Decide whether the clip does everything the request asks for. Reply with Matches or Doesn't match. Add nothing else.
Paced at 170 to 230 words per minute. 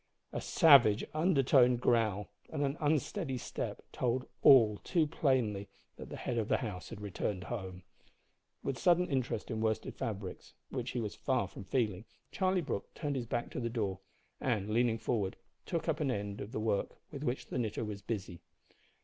Matches